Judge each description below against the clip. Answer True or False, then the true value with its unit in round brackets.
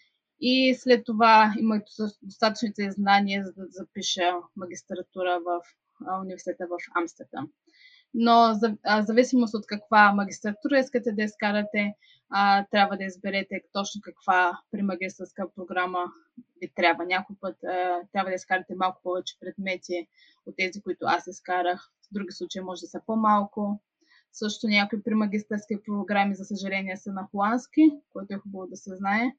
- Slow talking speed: False (135 wpm)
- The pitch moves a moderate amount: True (3.1 semitones)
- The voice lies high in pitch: True (200 Hz)